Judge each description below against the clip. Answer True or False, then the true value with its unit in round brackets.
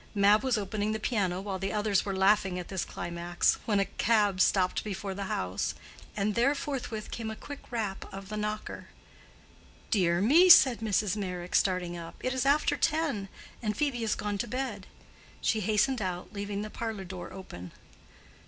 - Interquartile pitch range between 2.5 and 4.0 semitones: True (2.9 semitones)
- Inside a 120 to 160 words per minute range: False (180 wpm)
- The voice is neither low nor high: False (205 Hz)